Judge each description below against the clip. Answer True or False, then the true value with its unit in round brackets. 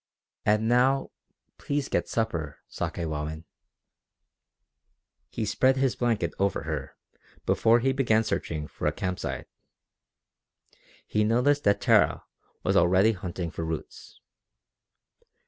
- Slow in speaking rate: True (110 wpm)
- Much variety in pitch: True (6.5 semitones)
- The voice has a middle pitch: False (105 Hz)